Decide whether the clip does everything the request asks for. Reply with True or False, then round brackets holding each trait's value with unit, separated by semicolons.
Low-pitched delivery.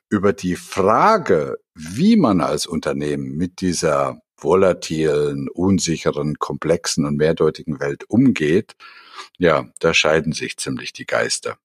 True (85 Hz)